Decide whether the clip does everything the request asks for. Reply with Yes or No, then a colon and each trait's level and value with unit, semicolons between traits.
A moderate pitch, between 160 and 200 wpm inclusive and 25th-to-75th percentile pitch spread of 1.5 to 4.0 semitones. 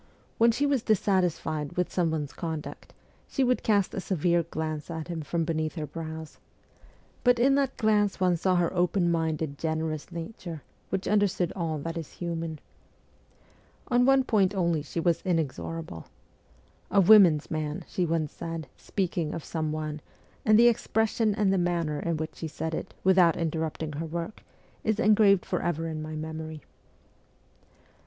Yes: medium, 170 Hz; average, 165 wpm; average, 3.6 semitones